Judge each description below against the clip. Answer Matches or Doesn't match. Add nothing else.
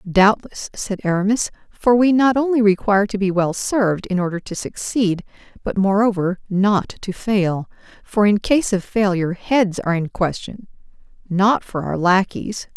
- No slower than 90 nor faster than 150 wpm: Doesn't match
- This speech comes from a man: Doesn't match